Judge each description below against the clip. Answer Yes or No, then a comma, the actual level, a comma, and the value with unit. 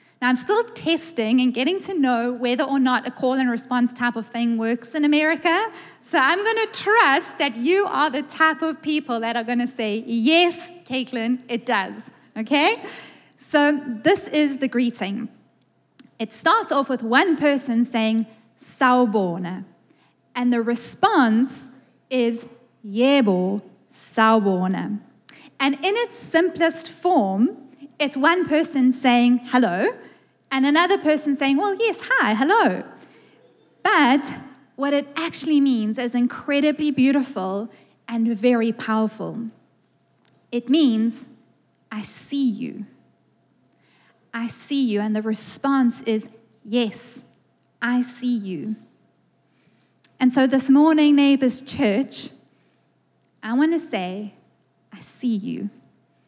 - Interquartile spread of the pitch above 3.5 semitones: Yes, average, 4.1 semitones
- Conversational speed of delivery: No, slow, 130 wpm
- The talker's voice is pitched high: Yes, very high, 255 Hz